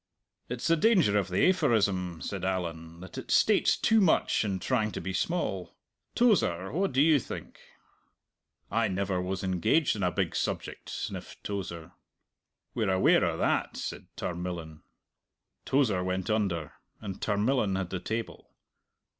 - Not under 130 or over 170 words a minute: Yes, average, 145 wpm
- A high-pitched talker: No, very low, 95 Hz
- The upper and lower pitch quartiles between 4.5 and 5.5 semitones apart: Yes, average, 4.8 semitones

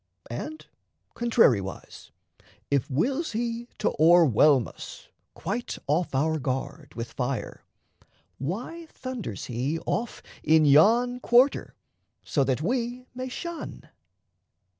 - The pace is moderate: No, slow, 105 wpm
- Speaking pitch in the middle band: Yes, medium, 175 Hz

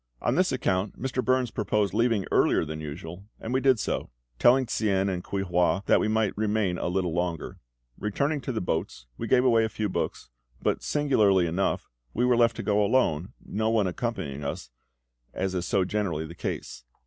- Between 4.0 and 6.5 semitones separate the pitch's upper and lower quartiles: Yes, average, 4.6 semitones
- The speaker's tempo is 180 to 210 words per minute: Yes, average, 190 wpm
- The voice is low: Yes, low, 100 Hz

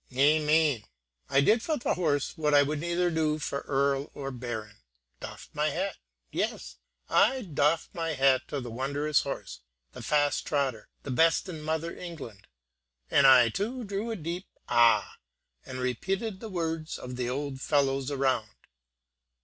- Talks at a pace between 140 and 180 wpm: Yes, average, 155 wpm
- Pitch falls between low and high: Yes, medium, 145 Hz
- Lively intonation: No, average, 3.9 semitones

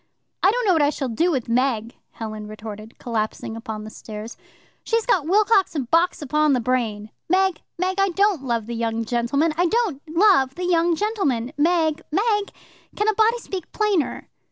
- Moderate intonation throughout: No, wide, 8.6 semitones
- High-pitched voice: Yes, very high, 305 Hz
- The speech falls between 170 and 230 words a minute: Yes, average, 180 wpm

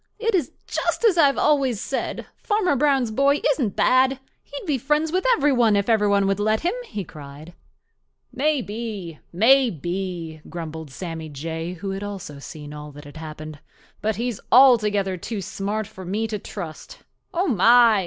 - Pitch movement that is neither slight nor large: No, wide, 7.8 semitones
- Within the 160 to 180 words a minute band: Yes, average, 165 wpm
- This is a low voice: No, high, 210 Hz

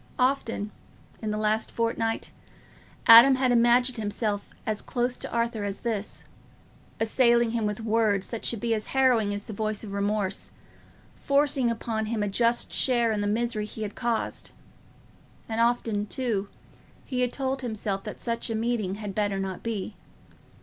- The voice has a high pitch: Yes, high, 225 Hz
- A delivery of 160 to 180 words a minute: Yes, average, 165 wpm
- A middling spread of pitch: No, narrow, 2.3 semitones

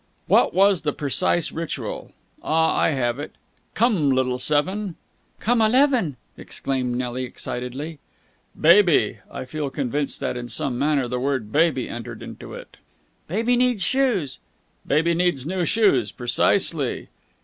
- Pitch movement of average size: No, wide, 6.3 semitones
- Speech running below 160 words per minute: Yes, average, 140 wpm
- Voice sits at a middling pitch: Yes, medium, 150 Hz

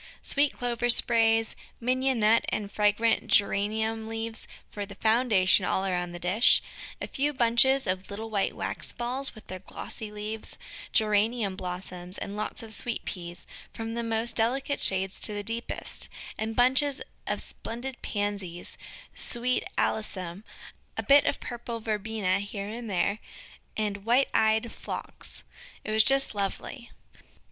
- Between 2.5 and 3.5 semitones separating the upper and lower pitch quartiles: Yes, average, 2.9 semitones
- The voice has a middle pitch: No, high, 220 Hz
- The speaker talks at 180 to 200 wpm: No, average, 145 wpm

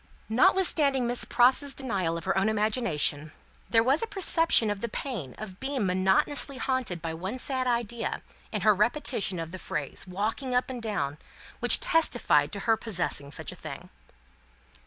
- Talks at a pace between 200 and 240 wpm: No, average, 165 wpm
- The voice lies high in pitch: Yes, high, 225 Hz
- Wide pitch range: Yes, wide, 5.8 semitones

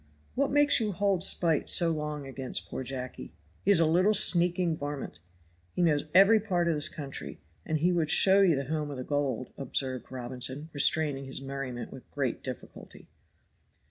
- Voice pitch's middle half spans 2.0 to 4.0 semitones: No, average, 4.7 semitones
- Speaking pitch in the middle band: Yes, medium, 150 Hz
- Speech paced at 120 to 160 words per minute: No, average, 175 wpm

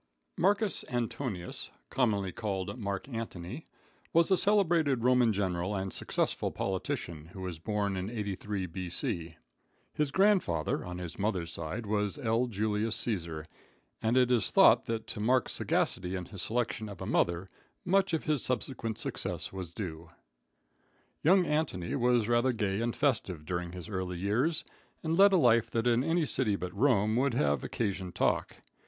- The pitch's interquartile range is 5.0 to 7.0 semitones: Yes, wide, 5.5 semitones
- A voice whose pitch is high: No, low, 110 Hz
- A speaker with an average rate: Yes, average, 160 wpm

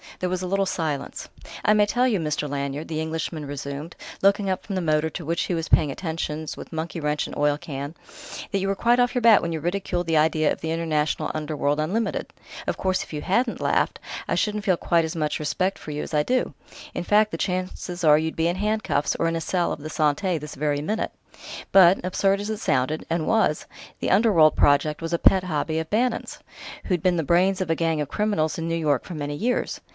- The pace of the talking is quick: Yes, fast, 230 wpm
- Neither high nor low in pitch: Yes, medium, 165 Hz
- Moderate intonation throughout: Yes, average, 4.1 semitones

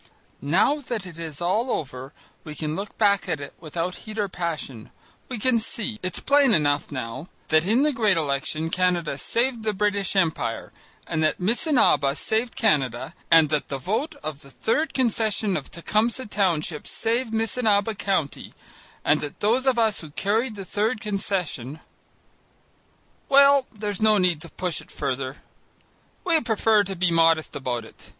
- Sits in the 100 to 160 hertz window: No, high, 195 Hz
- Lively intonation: Yes, wide, 6.2 semitones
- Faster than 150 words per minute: Yes, average, 165 wpm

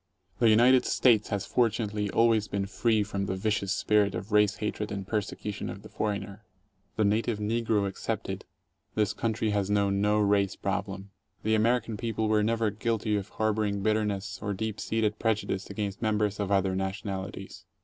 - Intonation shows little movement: Yes, narrow, 1.6 semitones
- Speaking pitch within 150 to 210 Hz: No, low, 105 Hz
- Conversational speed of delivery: Yes, average, 165 wpm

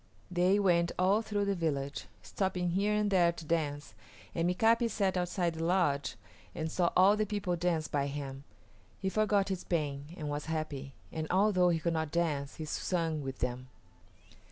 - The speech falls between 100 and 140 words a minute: No, average, 180 wpm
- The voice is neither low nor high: Yes, medium, 170 Hz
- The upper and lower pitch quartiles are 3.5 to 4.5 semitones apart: Yes, average, 4.1 semitones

